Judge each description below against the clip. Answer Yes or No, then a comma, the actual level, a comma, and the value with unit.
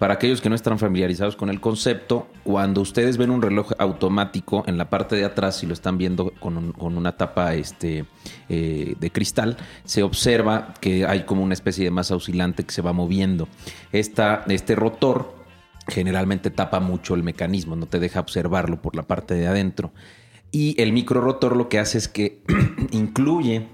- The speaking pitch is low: Yes, very low, 95 Hz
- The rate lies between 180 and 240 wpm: Yes, fast, 190 wpm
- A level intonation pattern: No, average, 3.6 semitones